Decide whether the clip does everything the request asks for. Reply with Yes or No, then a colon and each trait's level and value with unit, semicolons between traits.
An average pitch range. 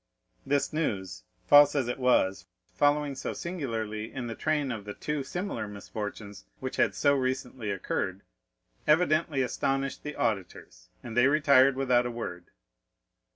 Yes: average, 4.9 semitones